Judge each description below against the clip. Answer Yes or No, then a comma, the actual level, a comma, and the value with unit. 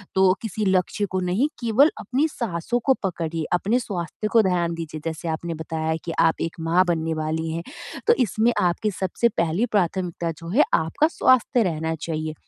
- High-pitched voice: No, medium, 180 Hz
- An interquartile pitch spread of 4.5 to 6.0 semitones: Yes, average, 5.0 semitones